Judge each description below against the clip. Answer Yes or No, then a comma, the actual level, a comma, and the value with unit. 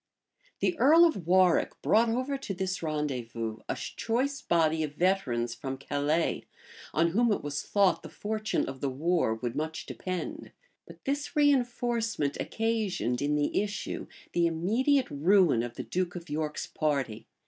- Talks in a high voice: No, medium, 175 Hz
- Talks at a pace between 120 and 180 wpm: Yes, average, 160 wpm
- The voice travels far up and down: Yes, wide, 7.6 semitones